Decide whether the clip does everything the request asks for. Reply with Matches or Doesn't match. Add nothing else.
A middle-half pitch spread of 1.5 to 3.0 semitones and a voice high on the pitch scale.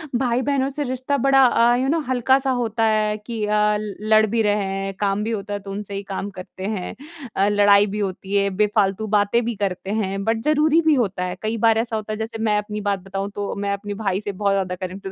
Matches